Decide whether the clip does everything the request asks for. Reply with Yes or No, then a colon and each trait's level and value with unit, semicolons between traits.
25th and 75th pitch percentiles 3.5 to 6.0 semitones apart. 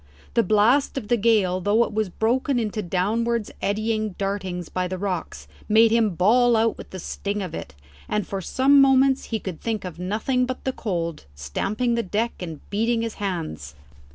Yes: average, 4.0 semitones